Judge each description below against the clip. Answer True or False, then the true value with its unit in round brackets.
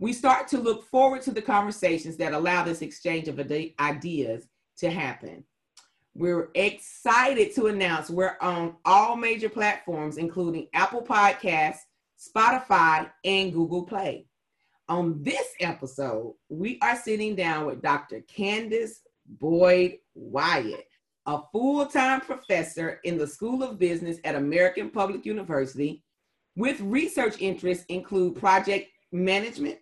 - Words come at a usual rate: False (125 wpm)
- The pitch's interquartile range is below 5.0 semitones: False (5.3 semitones)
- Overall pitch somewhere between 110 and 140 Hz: False (185 Hz)